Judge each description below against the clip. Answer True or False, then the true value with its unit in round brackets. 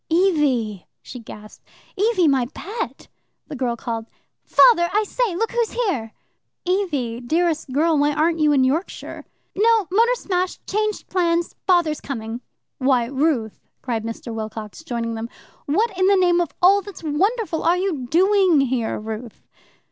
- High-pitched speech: True (320 Hz)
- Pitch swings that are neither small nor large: False (7.7 semitones)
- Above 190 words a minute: False (155 wpm)